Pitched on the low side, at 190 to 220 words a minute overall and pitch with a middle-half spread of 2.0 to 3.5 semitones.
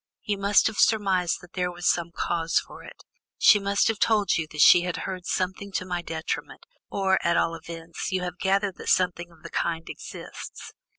No: medium, 180 Hz; average, 200 wpm; narrow, 2.6 semitones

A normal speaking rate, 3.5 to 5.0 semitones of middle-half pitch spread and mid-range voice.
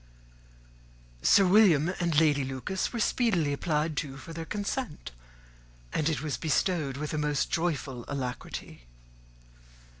No: slow, 125 wpm; average, 3.8 semitones; medium, 155 Hz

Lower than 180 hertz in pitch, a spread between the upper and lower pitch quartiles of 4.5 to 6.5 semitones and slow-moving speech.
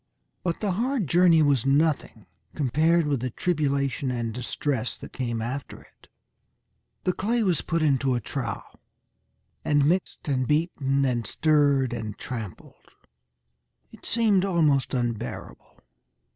Yes: medium, 140 Hz; average, 4.9 semitones; slow, 130 wpm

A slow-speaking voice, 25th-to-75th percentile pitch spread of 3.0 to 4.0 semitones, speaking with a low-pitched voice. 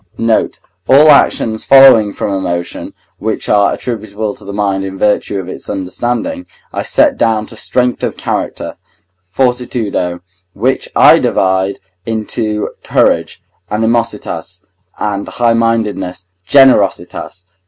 Yes: slow, 115 wpm; average, 3.6 semitones; low, 110 Hz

